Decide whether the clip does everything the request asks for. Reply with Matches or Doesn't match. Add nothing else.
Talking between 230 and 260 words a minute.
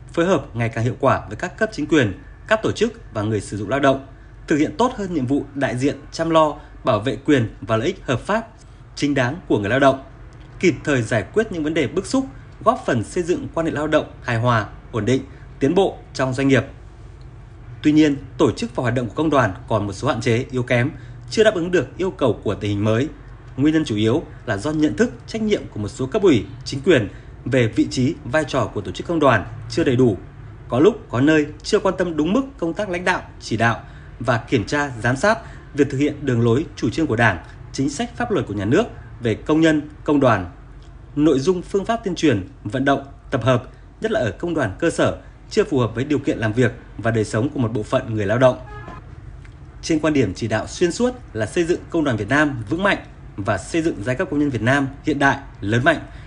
Matches